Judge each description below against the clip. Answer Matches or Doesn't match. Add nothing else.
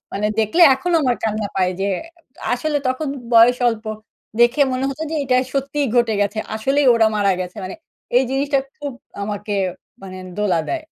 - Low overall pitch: Doesn't match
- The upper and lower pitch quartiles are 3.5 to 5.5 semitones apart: Matches